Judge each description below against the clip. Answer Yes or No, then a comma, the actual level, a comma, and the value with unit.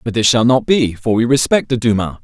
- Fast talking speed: Yes, fast, 270 wpm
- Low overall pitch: Yes, low, 115 Hz